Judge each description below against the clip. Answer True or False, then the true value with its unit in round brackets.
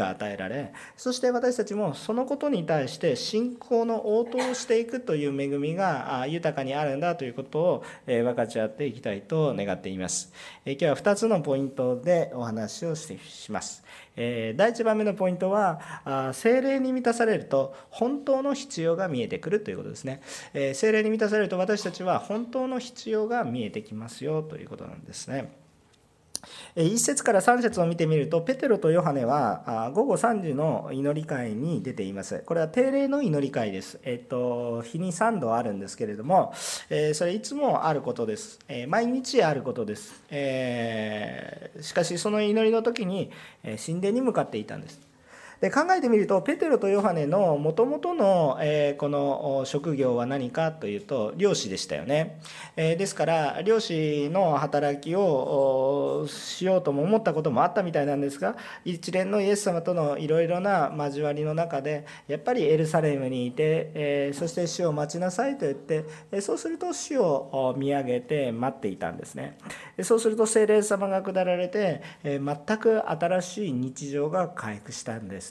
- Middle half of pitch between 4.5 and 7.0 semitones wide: False (7.6 semitones)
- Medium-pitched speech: True (165 Hz)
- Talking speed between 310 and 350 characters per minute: True (330 characters per minute)